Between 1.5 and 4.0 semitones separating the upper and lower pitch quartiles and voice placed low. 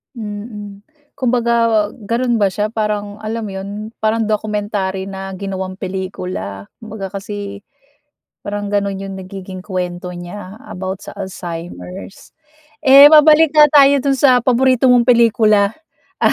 No: average, 3.2 semitones; high, 205 Hz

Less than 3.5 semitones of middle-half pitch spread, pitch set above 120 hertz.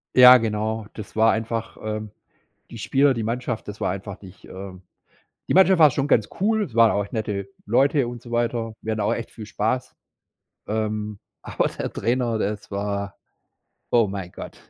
No: narrow, 2.6 semitones; low, 110 Hz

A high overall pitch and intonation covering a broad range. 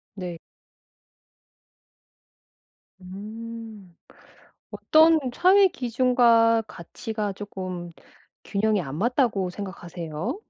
No: high, 215 Hz; average, 4.3 semitones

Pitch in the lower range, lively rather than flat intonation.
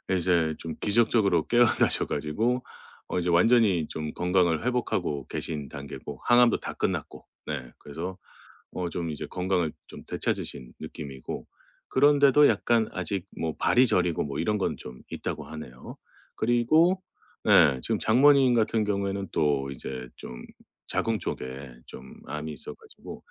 Yes: very low, 90 Hz; wide, 7.5 semitones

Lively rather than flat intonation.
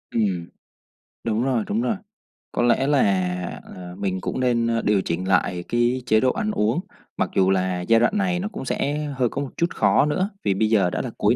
Yes: wide, 5.9 semitones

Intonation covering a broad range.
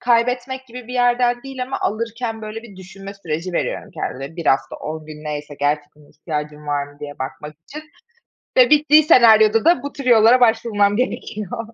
Yes: wide, 8.3 semitones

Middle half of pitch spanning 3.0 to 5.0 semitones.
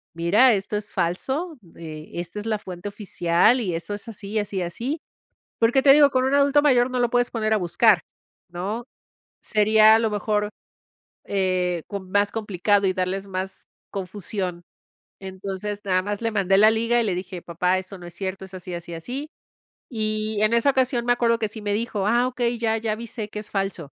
Yes: average, 3.7 semitones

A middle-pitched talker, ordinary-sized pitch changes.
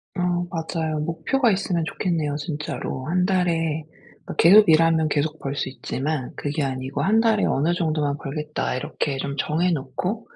Yes: medium, 160 Hz; average, 3.3 semitones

